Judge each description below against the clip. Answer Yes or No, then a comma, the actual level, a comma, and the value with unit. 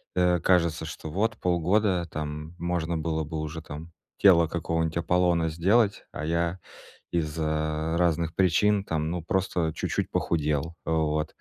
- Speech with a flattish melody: Yes, narrow, 2.1 semitones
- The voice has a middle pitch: No, very low, 85 Hz